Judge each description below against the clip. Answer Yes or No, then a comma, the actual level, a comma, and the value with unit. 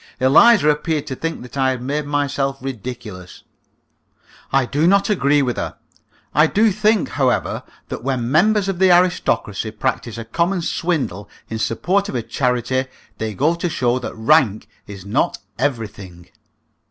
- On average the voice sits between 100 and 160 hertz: Yes, low, 135 Hz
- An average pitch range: No, wide, 6.2 semitones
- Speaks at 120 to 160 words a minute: Yes, average, 155 wpm